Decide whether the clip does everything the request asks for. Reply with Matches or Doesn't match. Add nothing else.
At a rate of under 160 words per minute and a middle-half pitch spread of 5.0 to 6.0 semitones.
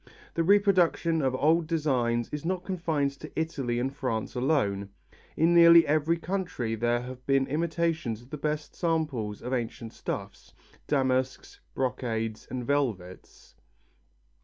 Matches